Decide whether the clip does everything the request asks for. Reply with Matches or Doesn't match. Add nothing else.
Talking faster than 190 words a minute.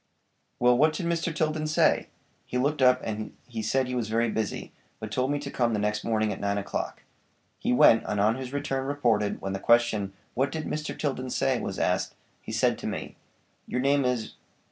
Matches